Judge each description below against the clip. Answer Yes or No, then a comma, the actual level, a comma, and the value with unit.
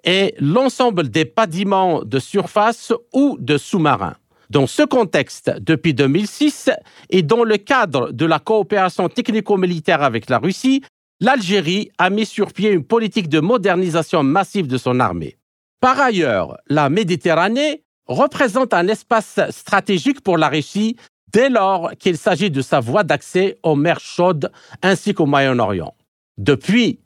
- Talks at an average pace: No, slow, 140 wpm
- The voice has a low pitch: No, high, 195 Hz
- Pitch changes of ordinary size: No, wide, 5.7 semitones